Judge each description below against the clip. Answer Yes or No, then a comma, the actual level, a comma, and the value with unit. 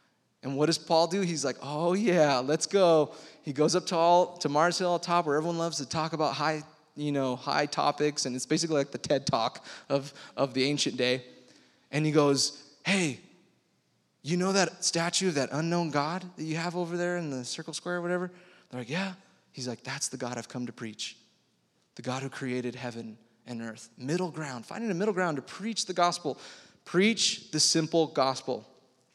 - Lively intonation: No, average, 4.7 semitones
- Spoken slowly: No, fast, 205 wpm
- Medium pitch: Yes, medium, 155 Hz